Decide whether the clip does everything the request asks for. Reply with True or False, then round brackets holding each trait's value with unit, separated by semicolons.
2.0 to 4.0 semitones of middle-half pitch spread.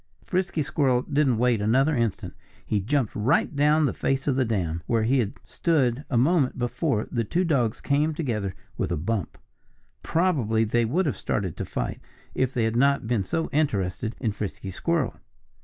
False (4.9 semitones)